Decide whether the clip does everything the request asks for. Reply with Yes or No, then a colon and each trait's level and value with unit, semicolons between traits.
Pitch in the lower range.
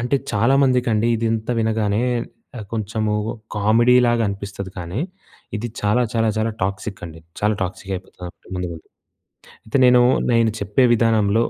Yes: low, 110 Hz